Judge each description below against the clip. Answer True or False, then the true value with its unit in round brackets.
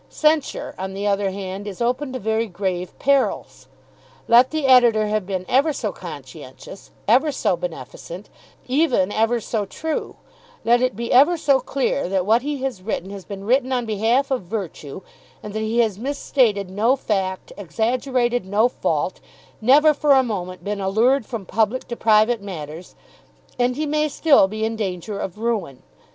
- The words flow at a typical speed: True (170 wpm)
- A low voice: False (225 Hz)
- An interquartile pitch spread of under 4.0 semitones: False (4.8 semitones)